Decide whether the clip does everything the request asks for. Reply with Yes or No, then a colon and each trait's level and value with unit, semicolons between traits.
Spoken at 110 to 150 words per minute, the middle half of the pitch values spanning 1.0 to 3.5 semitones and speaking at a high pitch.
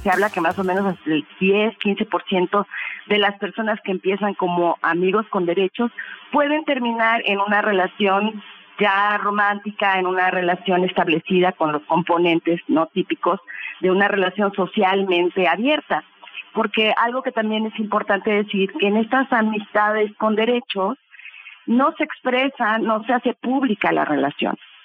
Yes: average, 145 wpm; average, 3.2 semitones; high, 200 Hz